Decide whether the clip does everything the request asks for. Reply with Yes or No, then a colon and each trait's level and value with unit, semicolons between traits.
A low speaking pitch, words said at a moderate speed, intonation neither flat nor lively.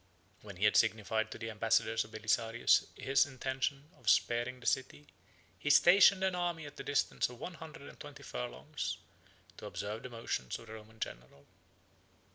Yes: low, 120 Hz; average, 175 wpm; average, 4.7 semitones